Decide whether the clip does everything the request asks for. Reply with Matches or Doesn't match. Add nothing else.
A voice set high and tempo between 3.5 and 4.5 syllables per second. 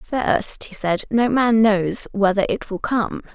Matches